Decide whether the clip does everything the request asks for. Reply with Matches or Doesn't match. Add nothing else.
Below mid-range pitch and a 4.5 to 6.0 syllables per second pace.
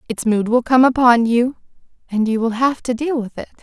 Doesn't match